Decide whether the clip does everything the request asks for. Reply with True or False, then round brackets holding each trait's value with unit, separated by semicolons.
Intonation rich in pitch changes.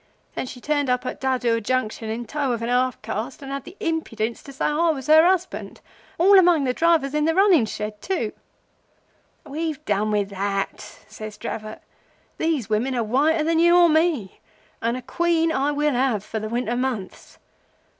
True (6.1 semitones)